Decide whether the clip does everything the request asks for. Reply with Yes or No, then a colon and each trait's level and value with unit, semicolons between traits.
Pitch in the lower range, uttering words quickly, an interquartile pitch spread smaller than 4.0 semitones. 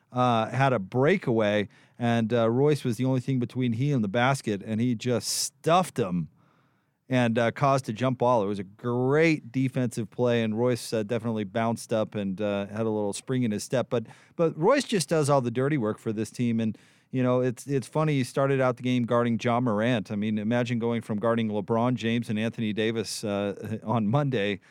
Yes: low, 120 Hz; fast, 215 wpm; average, 3.0 semitones